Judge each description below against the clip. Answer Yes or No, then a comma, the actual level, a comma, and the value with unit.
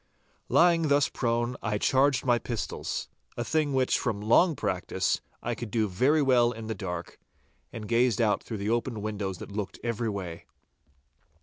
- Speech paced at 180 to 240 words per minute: No, average, 165 wpm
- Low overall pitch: Yes, low, 115 Hz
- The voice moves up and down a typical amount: Yes, average, 3.5 semitones